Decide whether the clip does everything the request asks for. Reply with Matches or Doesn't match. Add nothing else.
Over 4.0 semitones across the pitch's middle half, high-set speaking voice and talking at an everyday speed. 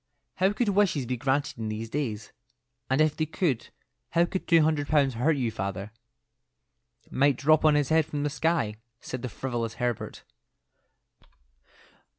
Doesn't match